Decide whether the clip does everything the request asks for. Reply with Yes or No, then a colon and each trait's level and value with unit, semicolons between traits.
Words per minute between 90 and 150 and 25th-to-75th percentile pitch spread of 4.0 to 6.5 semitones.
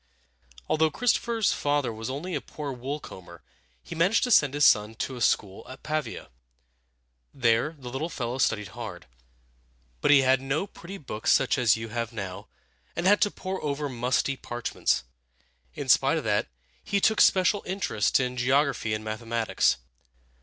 No: average, 165 wpm; average, 5.1 semitones